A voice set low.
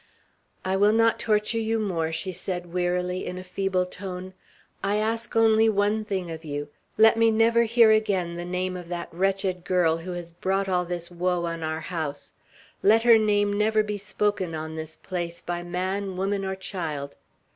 No: medium, 185 Hz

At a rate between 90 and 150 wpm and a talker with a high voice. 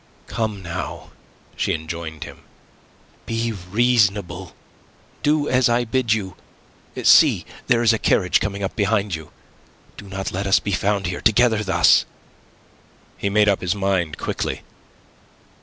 No: average, 140 wpm; low, 100 Hz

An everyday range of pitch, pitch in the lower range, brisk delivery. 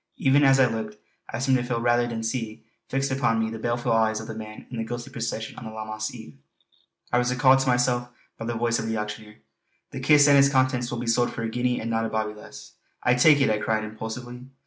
No: narrow, 2.2 semitones; low, 120 Hz; fast, 250 wpm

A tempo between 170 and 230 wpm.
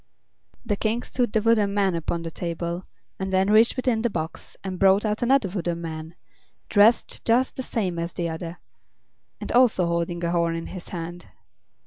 Yes: average, 180 wpm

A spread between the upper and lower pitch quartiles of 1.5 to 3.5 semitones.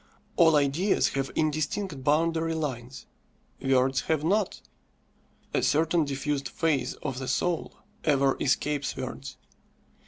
Yes: average, 3.2 semitones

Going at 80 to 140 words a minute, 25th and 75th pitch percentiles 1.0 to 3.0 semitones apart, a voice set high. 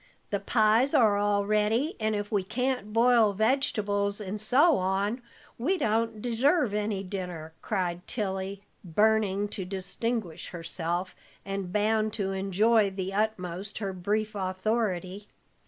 Yes: slow, 135 wpm; narrow, 2.5 semitones; high, 205 Hz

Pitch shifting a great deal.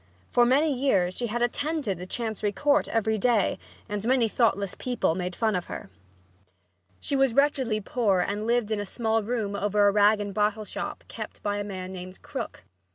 No: average, 3.2 semitones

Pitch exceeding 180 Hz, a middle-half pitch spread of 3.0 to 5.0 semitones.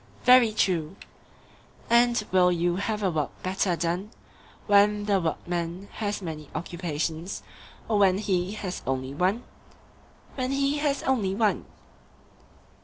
Yes: high, 190 Hz; average, 3.6 semitones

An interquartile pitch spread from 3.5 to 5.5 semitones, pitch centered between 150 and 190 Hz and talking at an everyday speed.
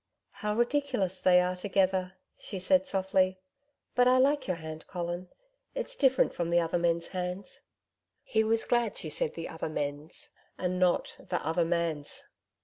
Yes: average, 4.3 semitones; medium, 185 Hz; average, 160 wpm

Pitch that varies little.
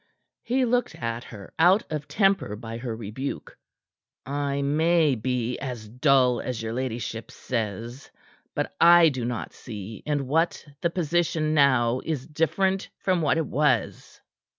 No: wide, 5.5 semitones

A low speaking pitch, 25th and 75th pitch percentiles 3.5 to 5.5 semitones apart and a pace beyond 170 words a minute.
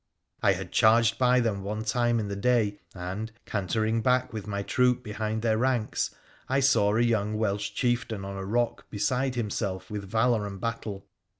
No: low, 110 Hz; average, 2.8 semitones; average, 180 wpm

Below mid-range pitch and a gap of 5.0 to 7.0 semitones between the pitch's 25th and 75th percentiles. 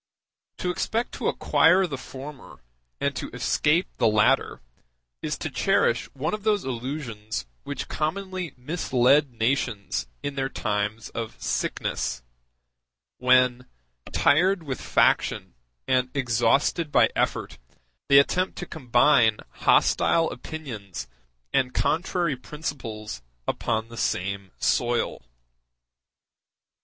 Yes: low, 130 Hz; wide, 5.5 semitones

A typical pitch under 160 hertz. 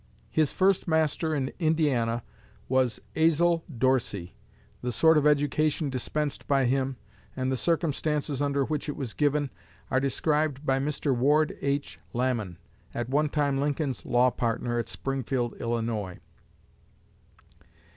Yes: medium, 140 Hz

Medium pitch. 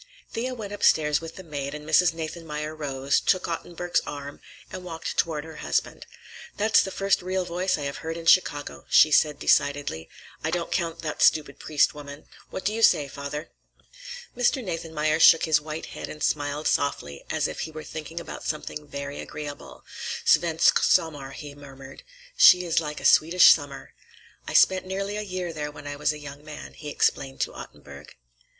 Yes: medium, 155 Hz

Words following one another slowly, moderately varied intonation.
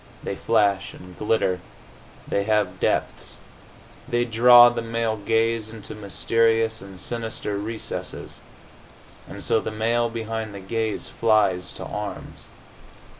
No: slow, 125 wpm; narrow, 1.9 semitones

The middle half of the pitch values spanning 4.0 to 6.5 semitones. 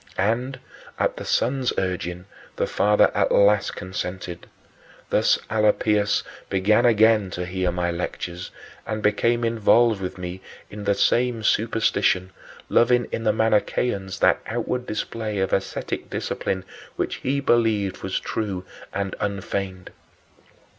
No: average, 3.3 semitones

